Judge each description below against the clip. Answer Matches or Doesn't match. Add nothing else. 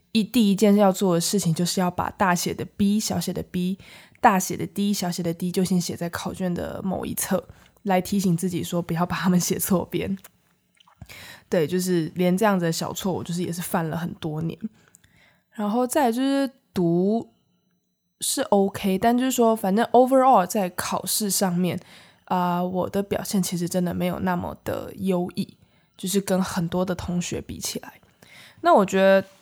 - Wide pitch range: Doesn't match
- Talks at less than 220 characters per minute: Doesn't match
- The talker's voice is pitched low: Doesn't match